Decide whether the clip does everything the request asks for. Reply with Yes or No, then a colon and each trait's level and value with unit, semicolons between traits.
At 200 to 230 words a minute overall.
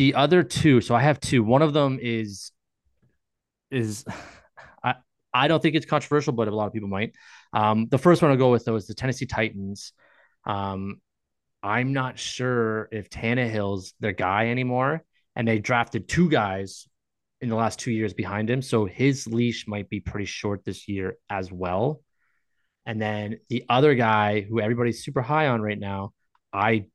No: average, 185 wpm